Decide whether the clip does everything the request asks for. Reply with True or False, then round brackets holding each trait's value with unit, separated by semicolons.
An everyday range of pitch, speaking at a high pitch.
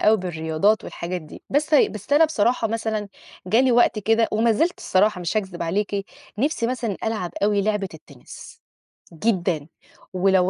True (3.9 semitones; 210 Hz)